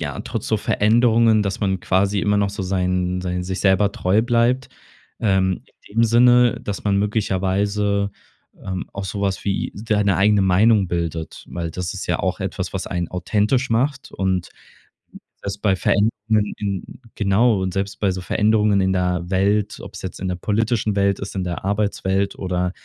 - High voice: No, low, 100 Hz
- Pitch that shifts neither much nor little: No, narrow, 2.2 semitones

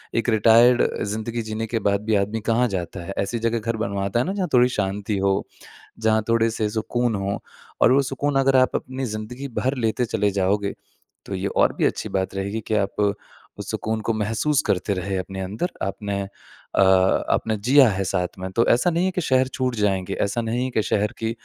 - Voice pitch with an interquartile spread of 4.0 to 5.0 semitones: No, average, 3.5 semitones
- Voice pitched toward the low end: Yes, low, 110 Hz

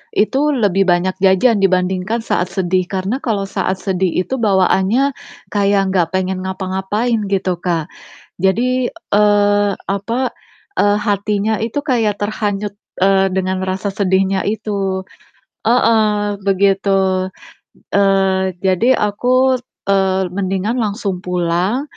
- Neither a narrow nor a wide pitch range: No, narrow, 1.9 semitones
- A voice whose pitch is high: Yes, high, 195 Hz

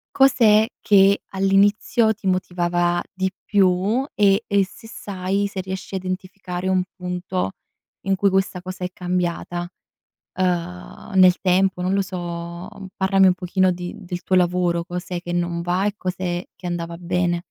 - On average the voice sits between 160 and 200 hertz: Yes, medium, 185 Hz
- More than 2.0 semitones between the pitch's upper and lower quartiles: No, narrow, 1.6 semitones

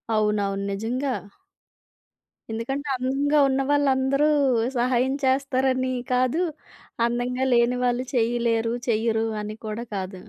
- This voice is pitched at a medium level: No, high, 245 Hz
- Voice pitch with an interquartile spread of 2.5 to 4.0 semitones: Yes, average, 2.8 semitones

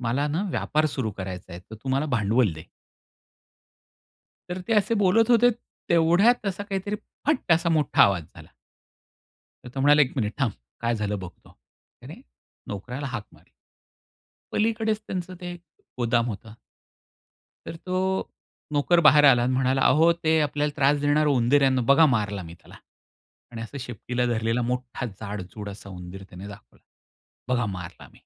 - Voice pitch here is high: No, low, 130 Hz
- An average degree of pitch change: No, wide, 7.0 semitones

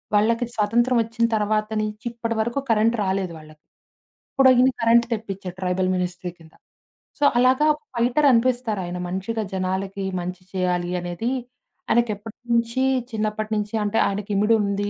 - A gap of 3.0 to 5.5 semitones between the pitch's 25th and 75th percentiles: Yes, average, 3.5 semitones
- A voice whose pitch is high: Yes, high, 215 Hz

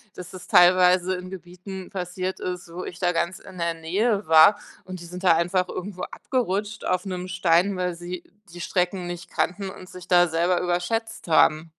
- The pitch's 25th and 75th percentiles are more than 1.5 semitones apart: No, narrow, 1.2 semitones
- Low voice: No, medium, 180 Hz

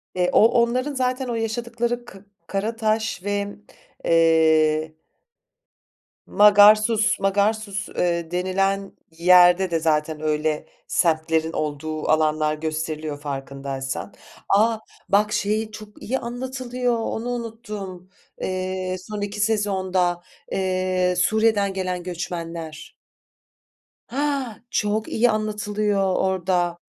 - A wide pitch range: No, average, 4.5 semitones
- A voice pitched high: Yes, high, 195 Hz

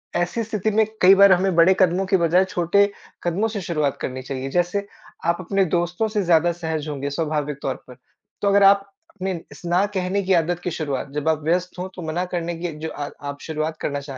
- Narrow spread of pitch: No, average, 3.4 semitones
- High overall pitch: No, medium, 175 Hz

